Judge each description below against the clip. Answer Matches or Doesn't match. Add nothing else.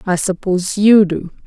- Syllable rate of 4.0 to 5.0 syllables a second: Matches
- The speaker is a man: Doesn't match